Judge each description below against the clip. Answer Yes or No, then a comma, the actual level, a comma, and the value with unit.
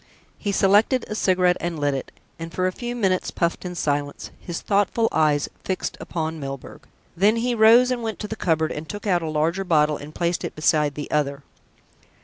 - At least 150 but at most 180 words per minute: No, average, 200 wpm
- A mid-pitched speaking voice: Yes, medium, 175 Hz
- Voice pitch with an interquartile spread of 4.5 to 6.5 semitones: Yes, average, 5.1 semitones